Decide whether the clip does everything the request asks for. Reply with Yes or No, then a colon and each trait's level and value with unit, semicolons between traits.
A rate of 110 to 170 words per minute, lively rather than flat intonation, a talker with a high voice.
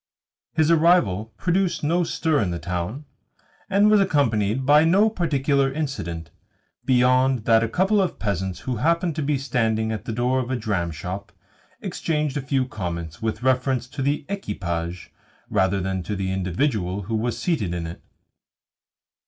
No: average, 160 wpm; wide, 7.6 semitones; low, 125 Hz